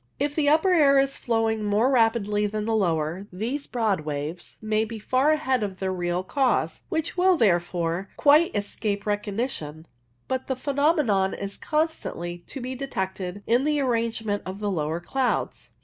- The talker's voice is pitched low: No, high, 220 Hz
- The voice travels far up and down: Yes, wide, 6.0 semitones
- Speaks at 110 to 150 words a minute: No, average, 165 wpm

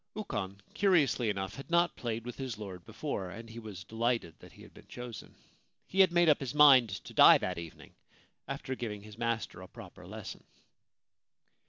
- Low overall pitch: Yes, low, 115 Hz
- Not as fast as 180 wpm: No, average, 185 wpm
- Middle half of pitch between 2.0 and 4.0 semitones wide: No, average, 5.1 semitones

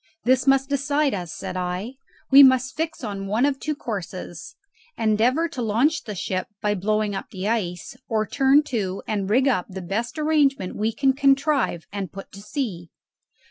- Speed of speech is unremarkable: Yes, average, 180 wpm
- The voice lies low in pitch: No, high, 225 Hz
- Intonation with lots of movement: Yes, wide, 5.8 semitones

